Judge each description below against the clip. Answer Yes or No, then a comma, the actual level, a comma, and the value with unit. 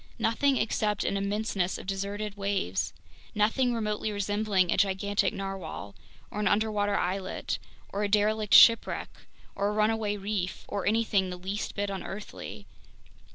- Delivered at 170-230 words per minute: No, average, 140 wpm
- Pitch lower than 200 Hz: No, high, 205 Hz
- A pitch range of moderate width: No, narrow, 1.5 semitones